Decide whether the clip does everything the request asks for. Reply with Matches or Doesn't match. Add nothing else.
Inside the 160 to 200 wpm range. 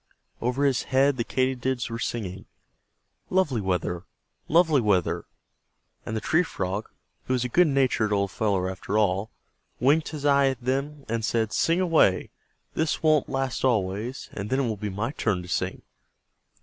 Matches